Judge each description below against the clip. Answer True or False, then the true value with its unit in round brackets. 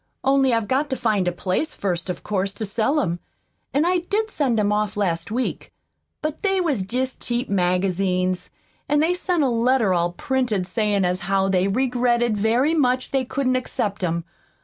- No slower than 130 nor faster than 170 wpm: False (185 wpm)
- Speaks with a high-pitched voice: True (230 Hz)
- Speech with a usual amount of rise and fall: False (5.7 semitones)